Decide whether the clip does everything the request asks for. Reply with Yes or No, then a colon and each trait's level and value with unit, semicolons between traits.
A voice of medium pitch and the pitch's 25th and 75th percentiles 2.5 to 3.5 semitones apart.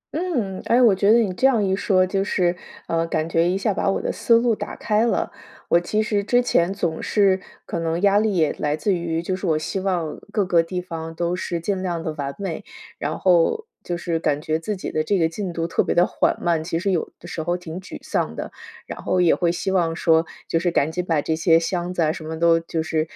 Yes: medium, 175 Hz; average, 2.9 semitones